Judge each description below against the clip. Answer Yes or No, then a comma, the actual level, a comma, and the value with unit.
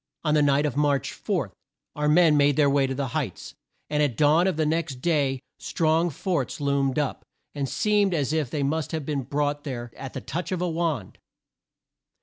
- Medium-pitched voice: Yes, medium, 150 Hz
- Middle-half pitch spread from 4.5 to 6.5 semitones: No, narrow, 2.6 semitones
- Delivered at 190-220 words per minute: Yes, average, 200 wpm